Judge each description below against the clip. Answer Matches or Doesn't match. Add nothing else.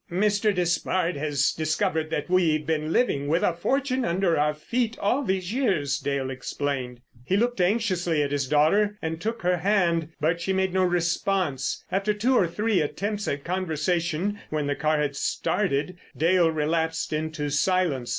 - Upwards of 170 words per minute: Doesn't match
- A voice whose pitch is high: Doesn't match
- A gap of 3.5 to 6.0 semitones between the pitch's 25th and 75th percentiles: Matches